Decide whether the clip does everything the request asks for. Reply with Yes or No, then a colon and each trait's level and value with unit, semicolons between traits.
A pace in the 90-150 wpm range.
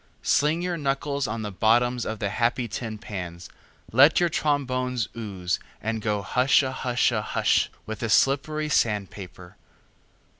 Yes: average, 140 wpm